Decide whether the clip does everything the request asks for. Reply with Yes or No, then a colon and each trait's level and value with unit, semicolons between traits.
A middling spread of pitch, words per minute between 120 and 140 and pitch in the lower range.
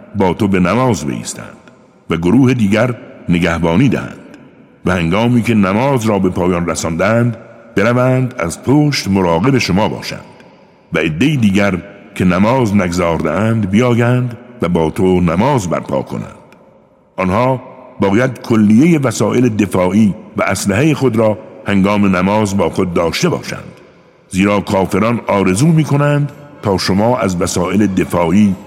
Yes: average, 4.8 semitones; average, 130 wpm; low, 105 Hz